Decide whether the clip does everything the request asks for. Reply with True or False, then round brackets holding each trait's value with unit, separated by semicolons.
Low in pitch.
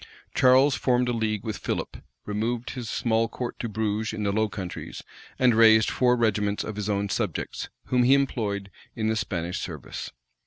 True (110 Hz)